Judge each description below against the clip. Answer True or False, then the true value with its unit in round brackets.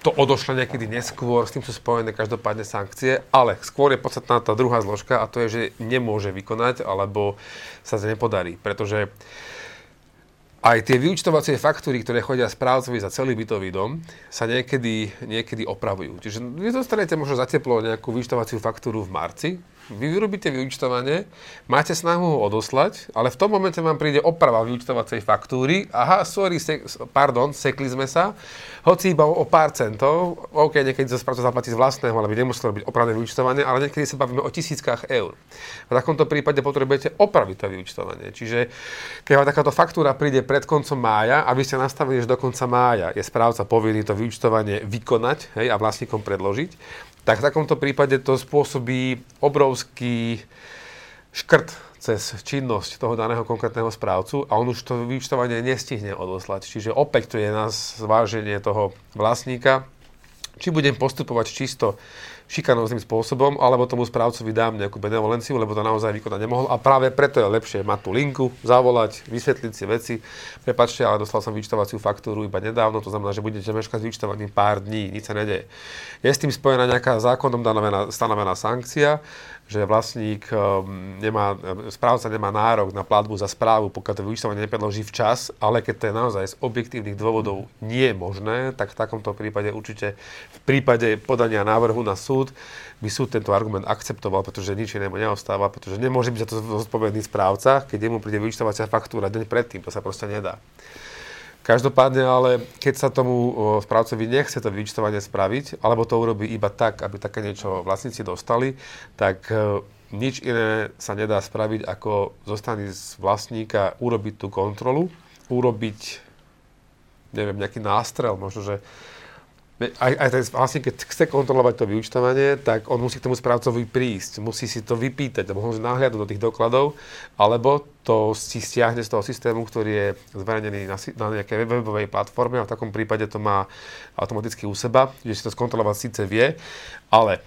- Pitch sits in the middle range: False (115 Hz)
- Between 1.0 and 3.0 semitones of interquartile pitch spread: False (3.6 semitones)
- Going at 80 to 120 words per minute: False (165 wpm)